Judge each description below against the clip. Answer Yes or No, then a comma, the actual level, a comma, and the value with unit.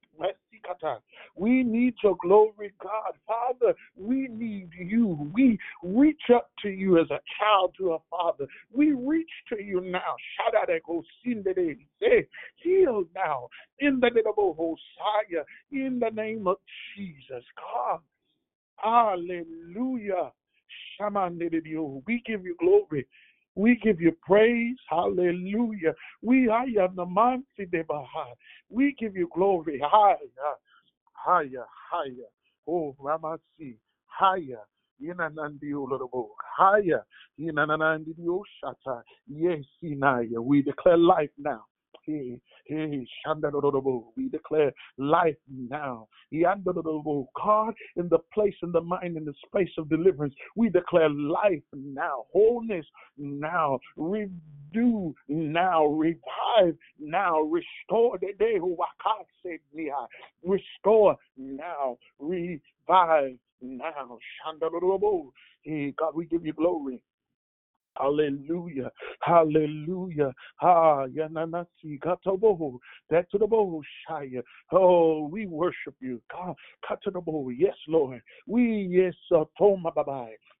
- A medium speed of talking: No, slow, 110 wpm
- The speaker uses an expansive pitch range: Yes, wide, 5.9 semitones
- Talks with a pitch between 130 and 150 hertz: No, medium, 175 Hz